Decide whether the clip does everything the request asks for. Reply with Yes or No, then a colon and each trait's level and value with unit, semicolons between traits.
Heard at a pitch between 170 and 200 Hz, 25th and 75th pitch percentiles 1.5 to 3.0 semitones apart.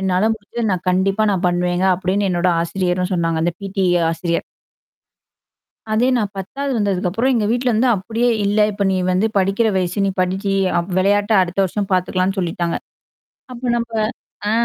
Yes: high, 190 Hz; average, 2.7 semitones